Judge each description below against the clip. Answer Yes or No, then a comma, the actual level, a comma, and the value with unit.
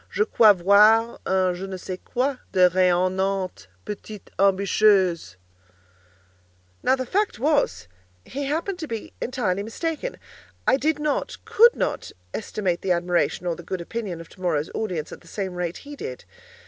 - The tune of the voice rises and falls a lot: Yes, wide, 5.9 semitones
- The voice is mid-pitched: No, high, 195 Hz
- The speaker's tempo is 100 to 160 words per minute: Yes, average, 150 wpm